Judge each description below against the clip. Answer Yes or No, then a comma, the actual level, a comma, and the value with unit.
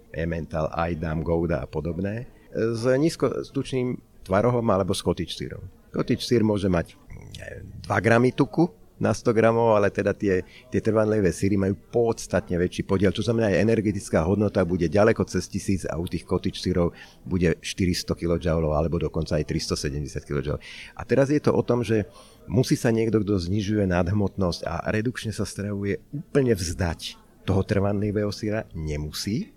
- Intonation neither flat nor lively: Yes, average, 4.1 semitones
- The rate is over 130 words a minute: Yes, average, 155 wpm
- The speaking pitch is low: Yes, low, 100 Hz